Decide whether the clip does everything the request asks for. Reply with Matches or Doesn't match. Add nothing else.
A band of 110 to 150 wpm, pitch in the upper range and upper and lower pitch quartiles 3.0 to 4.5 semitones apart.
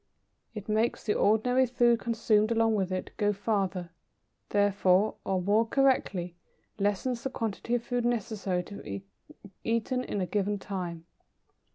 Matches